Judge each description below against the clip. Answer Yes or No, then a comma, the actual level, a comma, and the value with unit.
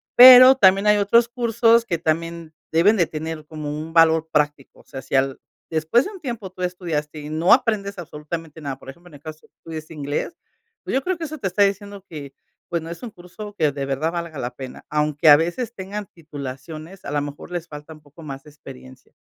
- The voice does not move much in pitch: No, average, 5.0 semitones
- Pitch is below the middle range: No, medium, 165 Hz